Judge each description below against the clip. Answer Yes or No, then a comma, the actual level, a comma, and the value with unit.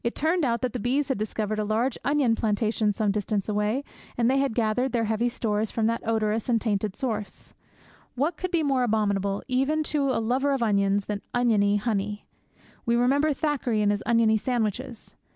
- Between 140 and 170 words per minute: No, average, 190 wpm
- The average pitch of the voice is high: Yes, high, 230 Hz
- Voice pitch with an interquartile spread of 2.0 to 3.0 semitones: No, average, 3.5 semitones